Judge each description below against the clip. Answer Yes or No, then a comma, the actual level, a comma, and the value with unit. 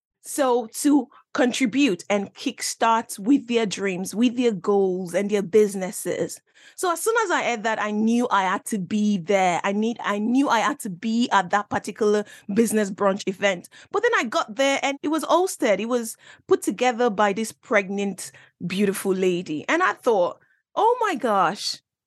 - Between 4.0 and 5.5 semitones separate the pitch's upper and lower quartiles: Yes, average, 4.7 semitones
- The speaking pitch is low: No, high, 220 Hz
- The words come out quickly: No, average, 180 wpm